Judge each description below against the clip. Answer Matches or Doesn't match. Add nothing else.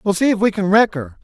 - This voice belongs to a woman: Doesn't match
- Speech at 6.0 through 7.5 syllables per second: Matches